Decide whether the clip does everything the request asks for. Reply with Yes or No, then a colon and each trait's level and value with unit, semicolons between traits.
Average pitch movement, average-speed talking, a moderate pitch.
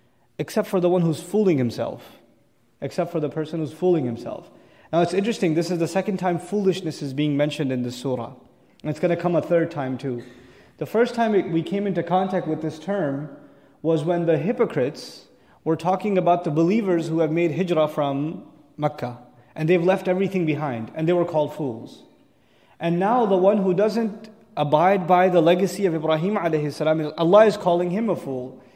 Yes: average, 3.8 semitones; average, 190 wpm; medium, 165 Hz